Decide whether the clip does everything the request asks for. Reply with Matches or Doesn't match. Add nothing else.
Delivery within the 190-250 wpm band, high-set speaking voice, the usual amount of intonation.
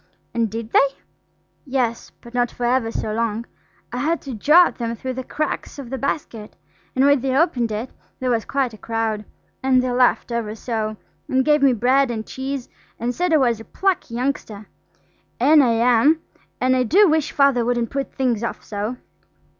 Matches